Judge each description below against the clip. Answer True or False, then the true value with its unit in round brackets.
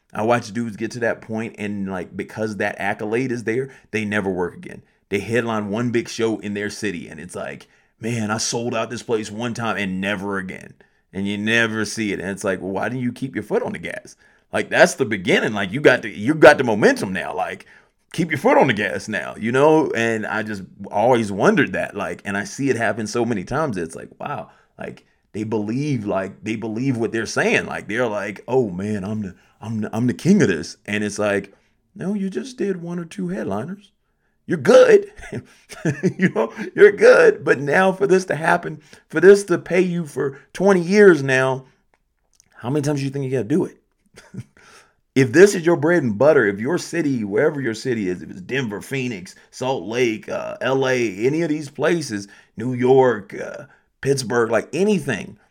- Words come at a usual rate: False (210 wpm)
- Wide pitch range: True (6.1 semitones)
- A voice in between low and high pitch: False (120 Hz)